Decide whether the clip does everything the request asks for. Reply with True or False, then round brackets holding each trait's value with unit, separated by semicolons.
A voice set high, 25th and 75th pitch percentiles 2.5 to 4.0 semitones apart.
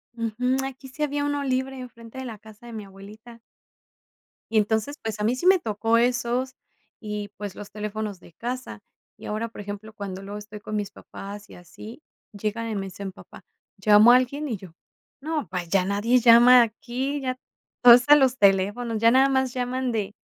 True (230 Hz; 3.6 semitones)